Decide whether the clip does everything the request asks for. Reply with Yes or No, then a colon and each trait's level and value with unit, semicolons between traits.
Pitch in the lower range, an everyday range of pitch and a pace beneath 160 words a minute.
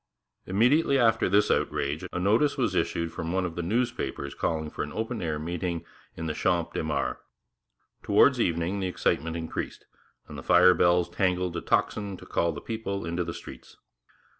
No: very low, 90 Hz; average, 3.4 semitones; average, 175 wpm